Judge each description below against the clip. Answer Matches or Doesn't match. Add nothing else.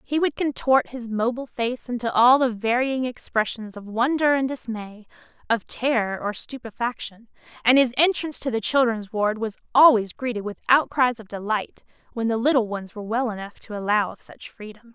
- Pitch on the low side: Doesn't match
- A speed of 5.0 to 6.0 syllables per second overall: Matches